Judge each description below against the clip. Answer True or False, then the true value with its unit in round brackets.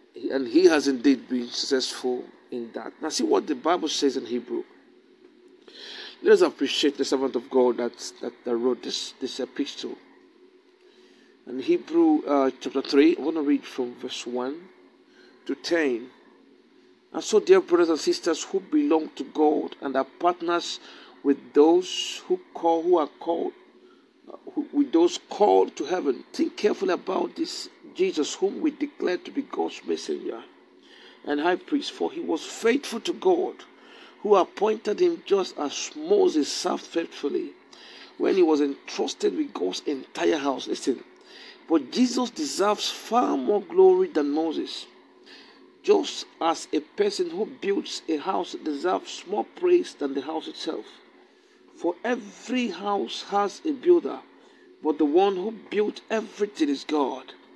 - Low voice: False (320 Hz)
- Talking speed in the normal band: True (150 wpm)